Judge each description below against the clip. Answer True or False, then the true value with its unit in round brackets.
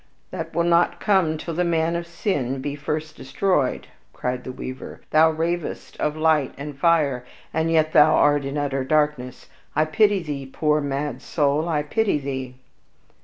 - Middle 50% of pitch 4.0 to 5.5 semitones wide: False (2.9 semitones)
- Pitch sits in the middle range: True (150 Hz)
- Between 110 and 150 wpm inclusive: False (170 wpm)